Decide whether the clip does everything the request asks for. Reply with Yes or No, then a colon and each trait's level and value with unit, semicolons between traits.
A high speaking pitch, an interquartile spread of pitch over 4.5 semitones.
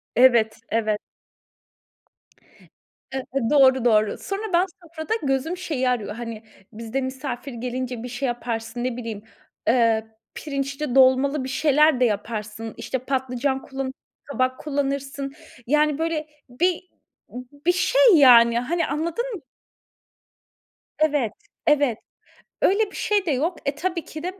No: very high, 265 Hz; average, 4.1 semitones